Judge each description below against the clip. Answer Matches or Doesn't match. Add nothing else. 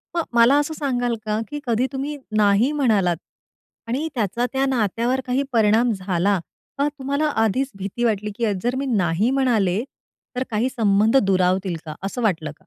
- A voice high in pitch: Matches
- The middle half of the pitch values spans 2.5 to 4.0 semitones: Doesn't match